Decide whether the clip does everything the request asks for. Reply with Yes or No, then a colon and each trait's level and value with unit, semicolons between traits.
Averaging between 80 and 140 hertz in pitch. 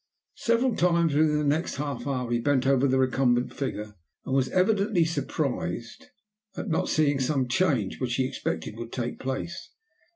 Yes: low, 135 Hz